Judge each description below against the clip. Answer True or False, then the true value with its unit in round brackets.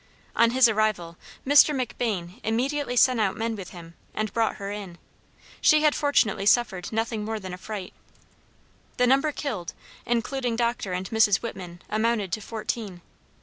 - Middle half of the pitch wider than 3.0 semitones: True (3.8 semitones)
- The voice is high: True (220 Hz)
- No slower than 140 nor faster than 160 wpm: True (150 wpm)